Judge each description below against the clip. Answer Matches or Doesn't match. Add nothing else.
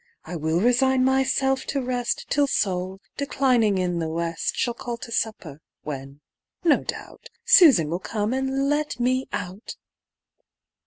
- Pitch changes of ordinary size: Doesn't match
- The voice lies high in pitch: Matches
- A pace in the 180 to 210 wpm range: Doesn't match